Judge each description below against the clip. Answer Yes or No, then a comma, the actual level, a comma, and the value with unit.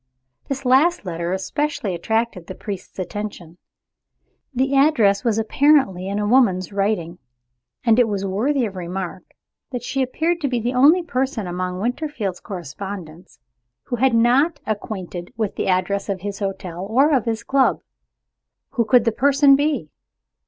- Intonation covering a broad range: Yes, wide, 5.8 semitones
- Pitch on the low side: No, high, 220 Hz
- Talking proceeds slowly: No, average, 150 wpm